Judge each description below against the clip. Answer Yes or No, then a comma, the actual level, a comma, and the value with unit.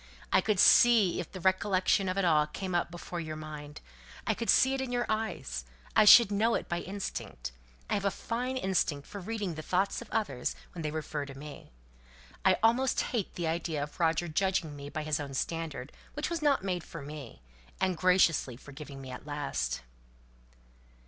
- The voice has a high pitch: No, medium, 175 Hz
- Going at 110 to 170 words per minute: No, average, 190 wpm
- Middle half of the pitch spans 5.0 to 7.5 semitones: Yes, average, 5.3 semitones